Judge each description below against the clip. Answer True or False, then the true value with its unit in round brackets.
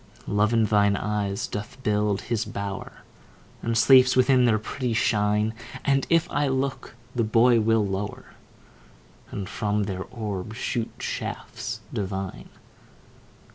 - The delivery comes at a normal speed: False (130 wpm)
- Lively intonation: False (2.9 semitones)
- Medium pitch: False (110 Hz)